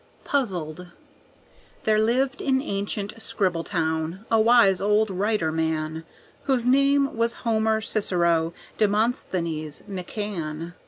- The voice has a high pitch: Yes, high, 205 Hz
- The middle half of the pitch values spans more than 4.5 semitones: Yes, average, 5.3 semitones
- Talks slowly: Yes, slow, 100 wpm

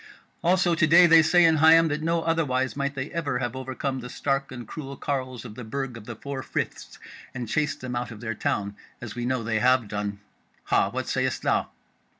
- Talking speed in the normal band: No, fast, 215 wpm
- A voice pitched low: Yes, low, 130 Hz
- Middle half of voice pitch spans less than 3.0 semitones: No, average, 4.3 semitones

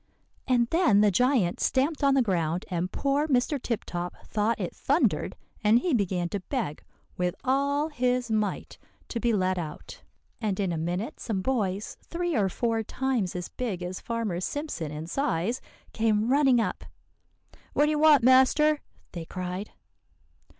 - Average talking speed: Yes, average, 165 wpm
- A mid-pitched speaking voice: No, high, 225 Hz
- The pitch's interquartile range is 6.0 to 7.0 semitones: Yes, wide, 6.4 semitones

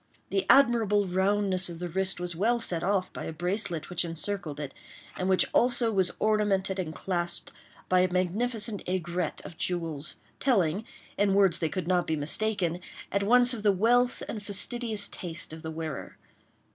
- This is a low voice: No, high, 190 Hz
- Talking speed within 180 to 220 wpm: No, average, 170 wpm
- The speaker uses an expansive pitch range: No, average, 3.4 semitones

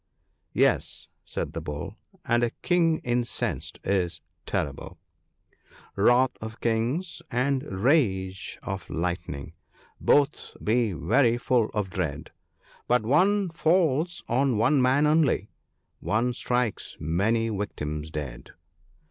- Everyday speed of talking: No, slow, 130 wpm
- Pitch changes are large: Yes, wide, 6.4 semitones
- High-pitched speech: No, low, 115 Hz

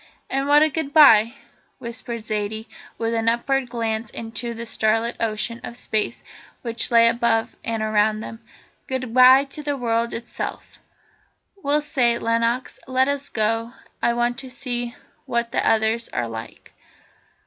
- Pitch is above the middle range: Yes, high, 235 Hz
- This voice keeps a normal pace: Yes, average, 150 wpm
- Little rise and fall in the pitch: Yes, narrow, 2.2 semitones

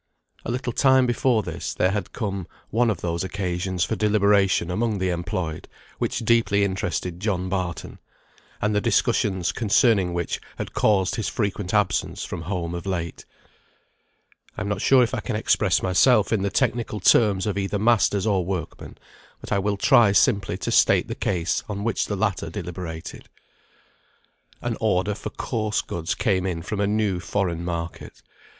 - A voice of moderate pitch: No, low, 100 Hz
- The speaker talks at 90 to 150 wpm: No, average, 170 wpm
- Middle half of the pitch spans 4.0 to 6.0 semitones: No, average, 3.0 semitones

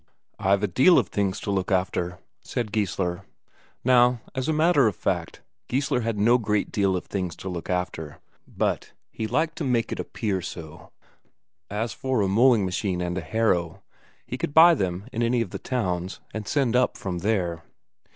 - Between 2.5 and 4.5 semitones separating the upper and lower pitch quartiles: No, average, 5.1 semitones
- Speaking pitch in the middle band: No, low, 105 Hz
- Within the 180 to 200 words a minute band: Yes, average, 185 wpm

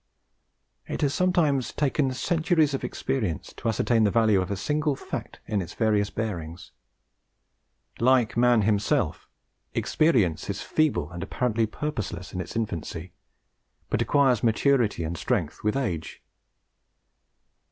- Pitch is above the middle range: No, low, 115 Hz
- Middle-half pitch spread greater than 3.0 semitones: Yes, wide, 5.6 semitones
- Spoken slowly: Yes, slow, 130 wpm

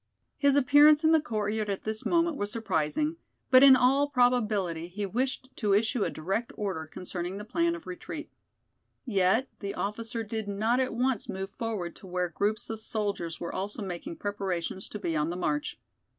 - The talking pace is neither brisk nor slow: Yes, average, 180 wpm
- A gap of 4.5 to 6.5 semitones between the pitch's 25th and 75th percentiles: Yes, average, 5.2 semitones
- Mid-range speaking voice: No, high, 215 Hz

